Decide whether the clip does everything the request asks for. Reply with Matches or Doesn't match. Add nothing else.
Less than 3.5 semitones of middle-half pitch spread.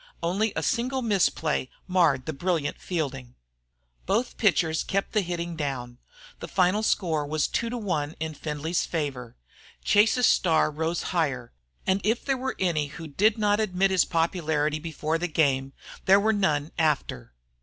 Doesn't match